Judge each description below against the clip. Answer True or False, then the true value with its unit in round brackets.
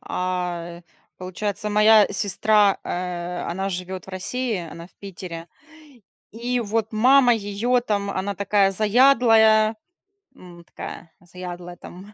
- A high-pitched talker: True (200 Hz)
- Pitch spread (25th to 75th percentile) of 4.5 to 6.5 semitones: False (3.3 semitones)